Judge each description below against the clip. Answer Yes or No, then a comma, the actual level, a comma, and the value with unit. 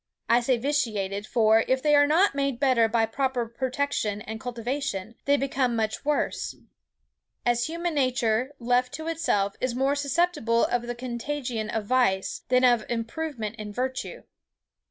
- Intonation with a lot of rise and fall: No, average, 3.7 semitones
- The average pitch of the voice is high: Yes, very high, 250 Hz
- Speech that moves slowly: No, average, 155 wpm